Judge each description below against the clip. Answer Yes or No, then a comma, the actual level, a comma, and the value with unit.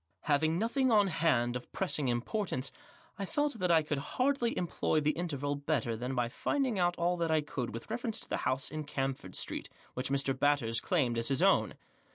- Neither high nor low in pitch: Yes, medium, 150 Hz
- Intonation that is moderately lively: No, wide, 5.7 semitones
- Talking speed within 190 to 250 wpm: Yes, average, 200 wpm